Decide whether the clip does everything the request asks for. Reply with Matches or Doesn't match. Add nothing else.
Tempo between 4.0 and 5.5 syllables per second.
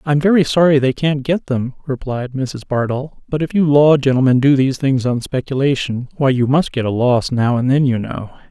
Matches